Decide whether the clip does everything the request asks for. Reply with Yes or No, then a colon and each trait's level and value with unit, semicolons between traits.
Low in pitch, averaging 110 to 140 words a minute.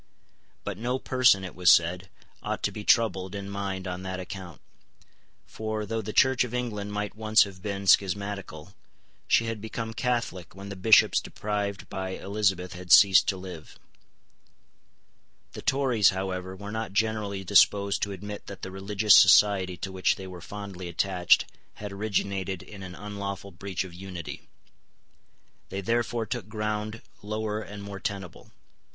No: low, 100 Hz; average, 155 wpm